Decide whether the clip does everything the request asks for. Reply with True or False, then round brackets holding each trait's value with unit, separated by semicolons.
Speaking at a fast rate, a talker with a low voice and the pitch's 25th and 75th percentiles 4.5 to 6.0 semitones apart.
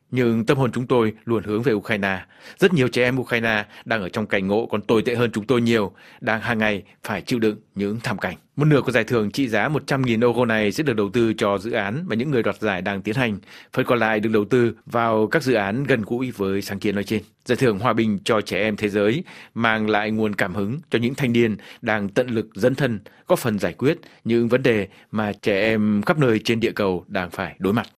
False (255 wpm; 115 Hz; 2.9 semitones)